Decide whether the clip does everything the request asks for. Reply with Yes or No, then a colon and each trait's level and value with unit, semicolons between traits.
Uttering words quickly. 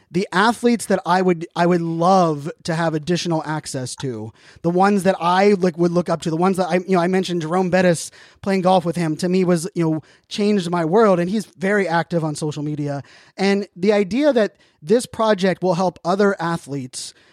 Yes: fast, 210 wpm